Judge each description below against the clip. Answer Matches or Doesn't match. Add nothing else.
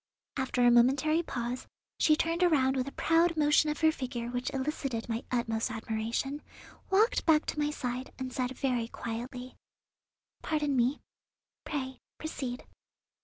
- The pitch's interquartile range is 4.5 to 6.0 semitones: Doesn't match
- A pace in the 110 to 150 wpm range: Matches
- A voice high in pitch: Matches